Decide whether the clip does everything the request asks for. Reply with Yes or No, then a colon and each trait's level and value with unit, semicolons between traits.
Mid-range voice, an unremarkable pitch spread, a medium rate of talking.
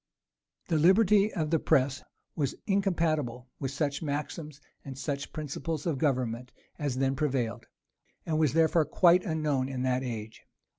Yes: medium, 145 Hz; average, 3.6 semitones; average, 145 wpm